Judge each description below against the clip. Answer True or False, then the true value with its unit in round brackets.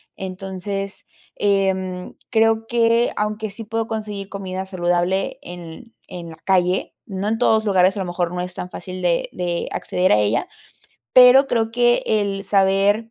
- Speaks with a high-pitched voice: True (195 Hz)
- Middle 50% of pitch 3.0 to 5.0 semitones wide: True (3.3 semitones)